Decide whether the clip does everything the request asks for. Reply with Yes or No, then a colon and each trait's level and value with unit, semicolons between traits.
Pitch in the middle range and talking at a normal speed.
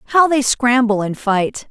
No: high, 240 Hz; average, 175 wpm